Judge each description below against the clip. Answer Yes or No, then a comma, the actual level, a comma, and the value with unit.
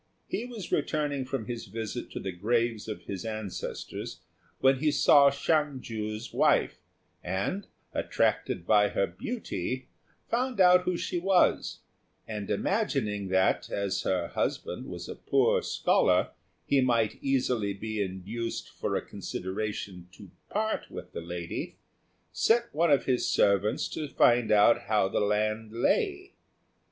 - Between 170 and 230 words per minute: No, average, 140 wpm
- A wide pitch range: Yes, wide, 6.2 semitones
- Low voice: Yes, low, 115 Hz